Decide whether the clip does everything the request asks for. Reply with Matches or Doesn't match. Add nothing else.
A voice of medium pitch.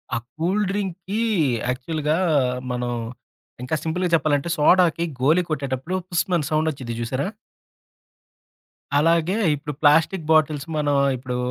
Matches